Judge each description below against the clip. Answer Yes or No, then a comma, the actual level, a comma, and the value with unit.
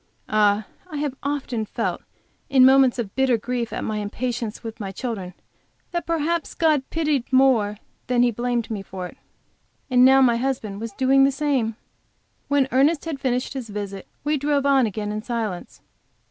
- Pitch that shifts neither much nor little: Yes, average, 4.1 semitones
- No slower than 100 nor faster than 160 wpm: No, average, 175 wpm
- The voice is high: Yes, very high, 250 Hz